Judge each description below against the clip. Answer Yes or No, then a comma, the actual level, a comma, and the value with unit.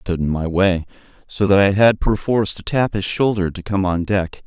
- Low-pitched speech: Yes, very low, 95 Hz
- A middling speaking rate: No, fast, 240 wpm